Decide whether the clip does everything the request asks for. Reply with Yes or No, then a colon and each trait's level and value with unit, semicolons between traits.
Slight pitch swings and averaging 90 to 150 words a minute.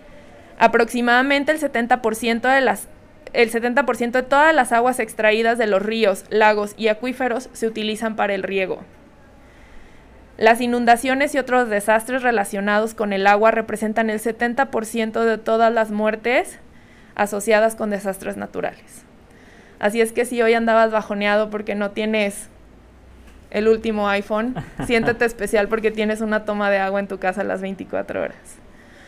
Yes: narrow, 2.3 semitones; average, 145 wpm